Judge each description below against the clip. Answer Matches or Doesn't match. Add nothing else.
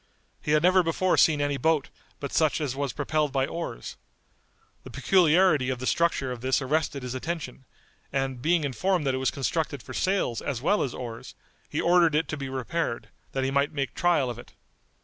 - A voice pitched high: Doesn't match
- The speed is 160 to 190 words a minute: Doesn't match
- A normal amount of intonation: Matches